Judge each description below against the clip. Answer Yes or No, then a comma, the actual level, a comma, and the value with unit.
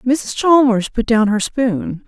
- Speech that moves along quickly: No, average, 175 wpm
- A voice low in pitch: No, high, 235 Hz